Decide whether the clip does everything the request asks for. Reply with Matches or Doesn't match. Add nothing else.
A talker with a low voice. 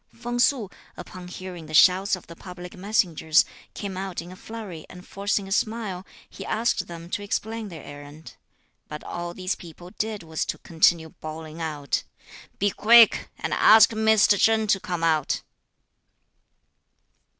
Doesn't match